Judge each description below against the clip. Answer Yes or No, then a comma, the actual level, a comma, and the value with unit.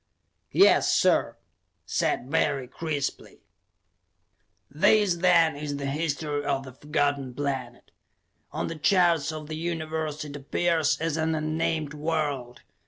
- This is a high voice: No, medium, 150 Hz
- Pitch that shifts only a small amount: Yes, narrow, 2.3 semitones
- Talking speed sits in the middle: No, slow, 120 wpm